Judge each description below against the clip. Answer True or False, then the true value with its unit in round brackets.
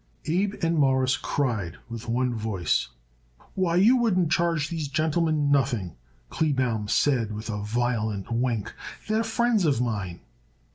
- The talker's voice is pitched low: True (130 Hz)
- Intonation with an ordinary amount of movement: False (6.8 semitones)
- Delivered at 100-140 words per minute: True (135 wpm)